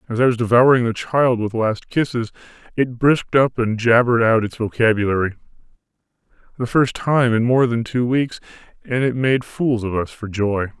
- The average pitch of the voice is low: Yes, low, 120 Hz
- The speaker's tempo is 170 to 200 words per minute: Yes, average, 185 wpm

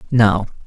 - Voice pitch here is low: Yes, low, 110 Hz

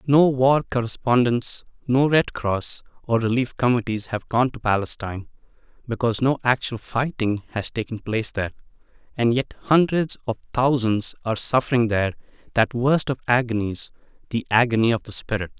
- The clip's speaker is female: No, male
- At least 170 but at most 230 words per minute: No, average, 145 wpm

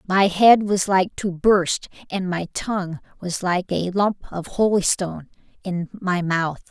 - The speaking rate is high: No, average, 160 wpm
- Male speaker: No, female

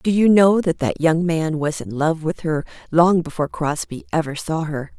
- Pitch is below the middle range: No, medium, 160 Hz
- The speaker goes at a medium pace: No, fast, 215 wpm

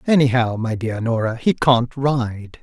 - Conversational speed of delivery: Yes, average, 160 wpm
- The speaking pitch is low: Yes, low, 120 Hz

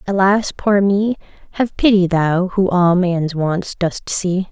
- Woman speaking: Yes, female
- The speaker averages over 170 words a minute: No, average, 160 wpm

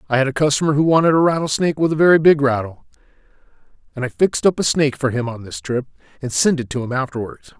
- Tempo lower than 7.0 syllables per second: No, 7.1 syllables/s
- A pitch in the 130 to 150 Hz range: Yes, medium, 140 Hz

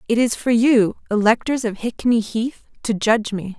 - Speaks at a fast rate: No, average, 185 wpm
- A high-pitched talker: Yes, high, 225 Hz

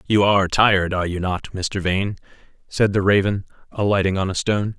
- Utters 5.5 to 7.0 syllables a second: Yes, 5.7 syllables/s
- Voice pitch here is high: No, very low, 95 Hz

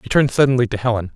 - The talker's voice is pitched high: No, low, 120 Hz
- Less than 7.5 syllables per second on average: No, 8.1 syllables/s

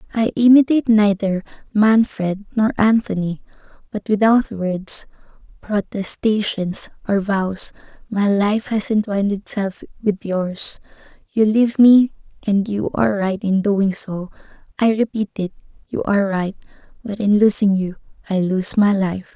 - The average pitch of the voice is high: Yes, high, 205 Hz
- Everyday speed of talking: No, slow, 130 wpm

